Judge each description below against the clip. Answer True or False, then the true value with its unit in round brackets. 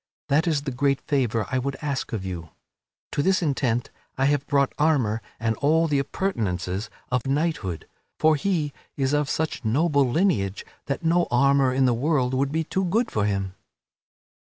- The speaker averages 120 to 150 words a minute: False (175 wpm)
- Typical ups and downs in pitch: True (4.5 semitones)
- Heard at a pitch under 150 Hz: True (140 Hz)